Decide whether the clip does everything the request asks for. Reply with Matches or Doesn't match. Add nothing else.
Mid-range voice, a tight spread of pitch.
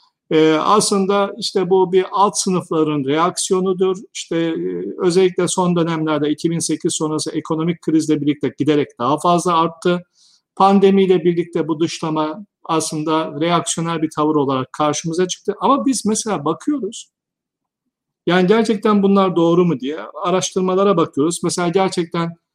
Doesn't match